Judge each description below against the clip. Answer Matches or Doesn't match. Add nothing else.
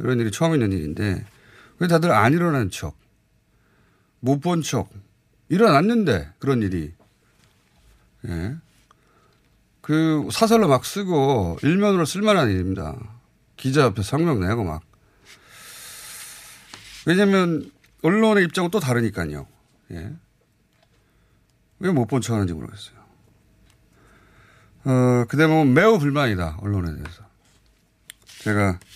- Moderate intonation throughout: Doesn't match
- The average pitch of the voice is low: Matches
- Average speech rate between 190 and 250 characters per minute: Matches